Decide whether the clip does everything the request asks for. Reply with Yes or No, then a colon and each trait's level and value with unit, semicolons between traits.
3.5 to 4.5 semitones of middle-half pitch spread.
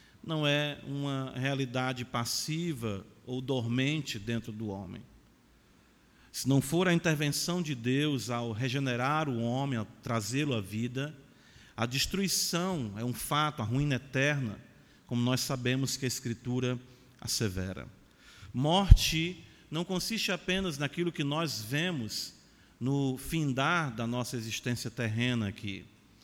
Yes: average, 4.0 semitones